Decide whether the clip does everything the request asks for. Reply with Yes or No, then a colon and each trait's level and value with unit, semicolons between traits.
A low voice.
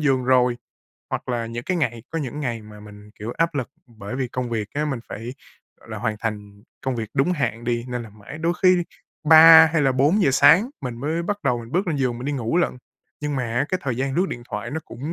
Yes: low, 130 Hz